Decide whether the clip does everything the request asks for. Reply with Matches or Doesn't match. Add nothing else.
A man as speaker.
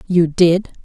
Doesn't match